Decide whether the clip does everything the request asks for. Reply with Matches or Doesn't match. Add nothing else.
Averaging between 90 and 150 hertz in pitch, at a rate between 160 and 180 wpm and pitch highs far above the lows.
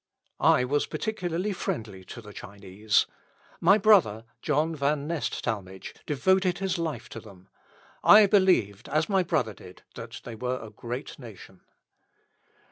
Doesn't match